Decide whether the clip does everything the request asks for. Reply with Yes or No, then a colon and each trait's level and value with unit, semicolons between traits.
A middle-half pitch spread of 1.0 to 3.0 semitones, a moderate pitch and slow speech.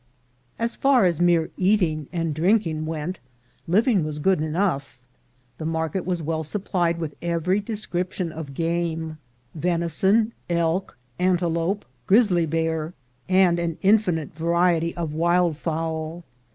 Yes: narrow, 2.5 semitones; medium, 170 Hz; slow, 130 wpm